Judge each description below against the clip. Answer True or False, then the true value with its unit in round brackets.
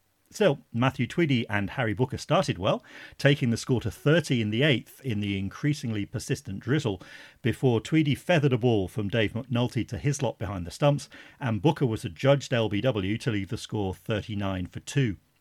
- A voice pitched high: False (120 Hz)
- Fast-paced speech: False (185 wpm)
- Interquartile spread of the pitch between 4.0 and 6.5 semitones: True (4.7 semitones)